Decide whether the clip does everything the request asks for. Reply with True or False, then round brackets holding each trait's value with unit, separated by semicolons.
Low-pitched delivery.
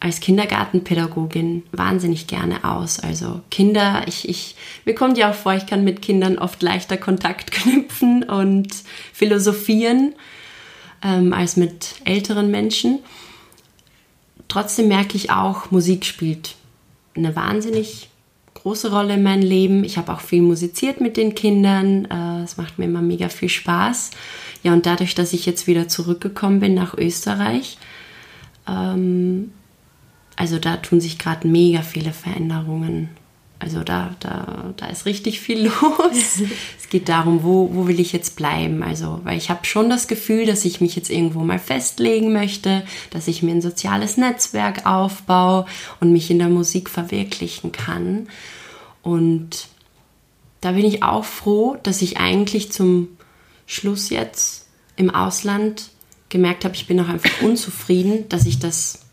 False (185 Hz)